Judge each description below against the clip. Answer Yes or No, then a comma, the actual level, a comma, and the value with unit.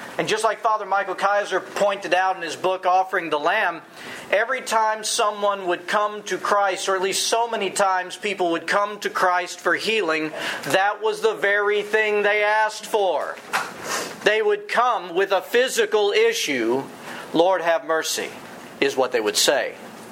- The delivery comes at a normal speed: Yes, average, 170 wpm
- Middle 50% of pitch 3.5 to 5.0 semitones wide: No, average, 2.9 semitones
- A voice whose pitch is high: Yes, high, 200 Hz